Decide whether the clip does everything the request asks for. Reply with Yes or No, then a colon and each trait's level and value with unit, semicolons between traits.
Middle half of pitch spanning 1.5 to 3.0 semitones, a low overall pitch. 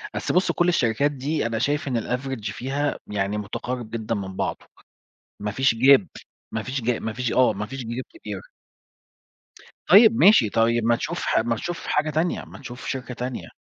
No: average, 3.8 semitones; low, 125 Hz